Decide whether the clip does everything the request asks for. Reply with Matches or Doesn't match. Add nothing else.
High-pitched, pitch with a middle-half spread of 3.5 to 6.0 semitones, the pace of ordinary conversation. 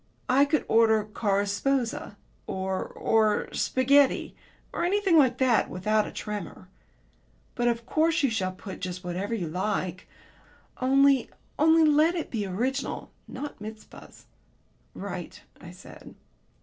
Doesn't match